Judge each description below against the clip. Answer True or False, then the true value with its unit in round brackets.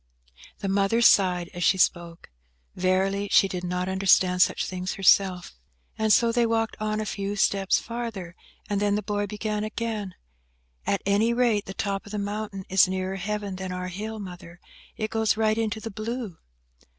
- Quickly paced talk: False (175 wpm)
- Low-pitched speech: False (200 Hz)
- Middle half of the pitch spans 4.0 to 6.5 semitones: False (2.5 semitones)